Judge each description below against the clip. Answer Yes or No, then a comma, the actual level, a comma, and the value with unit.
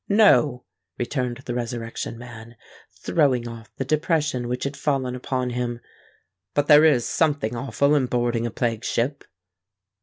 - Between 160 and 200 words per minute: No, average, 145 wpm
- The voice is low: Yes, low, 125 Hz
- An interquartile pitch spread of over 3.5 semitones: No, average, 3.2 semitones